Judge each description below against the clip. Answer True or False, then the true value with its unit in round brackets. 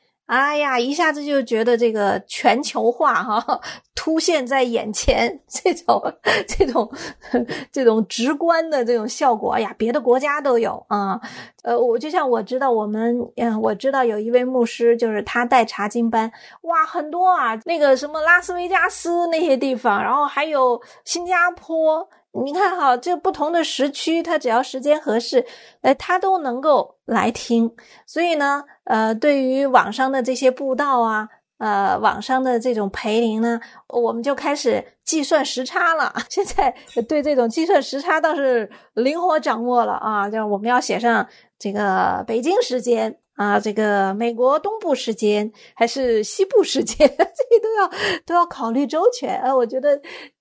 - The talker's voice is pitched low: False (265 Hz)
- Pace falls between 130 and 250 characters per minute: True (245 characters per minute)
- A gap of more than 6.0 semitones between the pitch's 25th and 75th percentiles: False (5.6 semitones)